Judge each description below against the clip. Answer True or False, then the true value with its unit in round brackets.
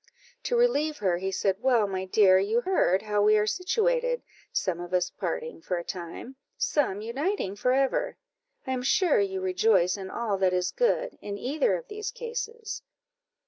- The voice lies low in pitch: False (225 Hz)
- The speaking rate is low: False (180 wpm)